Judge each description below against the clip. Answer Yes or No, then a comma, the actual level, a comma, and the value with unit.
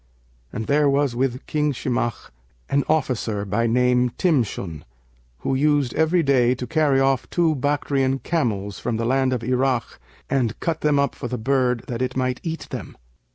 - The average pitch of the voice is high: No, low, 130 Hz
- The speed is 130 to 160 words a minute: No, average, 170 wpm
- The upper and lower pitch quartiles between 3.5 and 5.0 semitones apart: No, average, 3.1 semitones